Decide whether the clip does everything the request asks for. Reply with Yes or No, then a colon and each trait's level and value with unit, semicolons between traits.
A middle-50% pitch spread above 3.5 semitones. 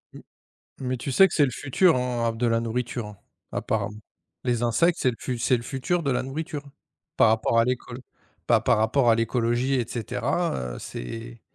No: average, 2.7 semitones